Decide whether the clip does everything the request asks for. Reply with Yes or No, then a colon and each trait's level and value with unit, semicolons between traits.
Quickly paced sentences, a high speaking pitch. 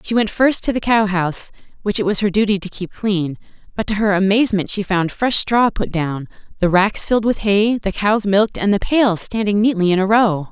Yes: fast, 235 wpm; high, 205 Hz